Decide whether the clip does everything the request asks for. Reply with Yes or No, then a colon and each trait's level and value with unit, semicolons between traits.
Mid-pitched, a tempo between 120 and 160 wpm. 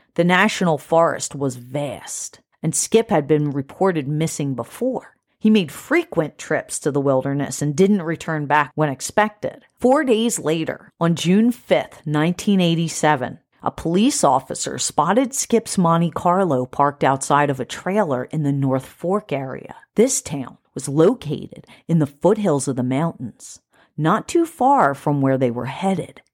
Yes: medium, 155 Hz; average, 155 wpm